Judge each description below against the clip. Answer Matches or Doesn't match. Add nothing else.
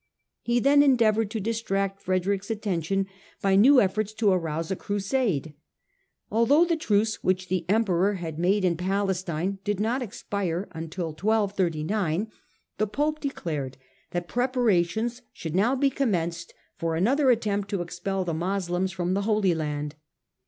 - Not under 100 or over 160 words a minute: Matches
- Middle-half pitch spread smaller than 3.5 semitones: Doesn't match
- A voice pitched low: Doesn't match